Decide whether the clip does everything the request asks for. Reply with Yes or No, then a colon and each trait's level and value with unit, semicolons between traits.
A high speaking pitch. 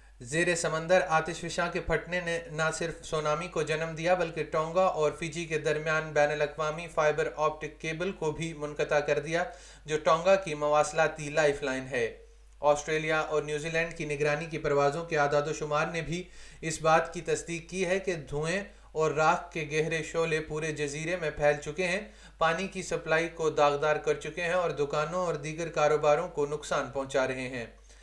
No: medium, 155 Hz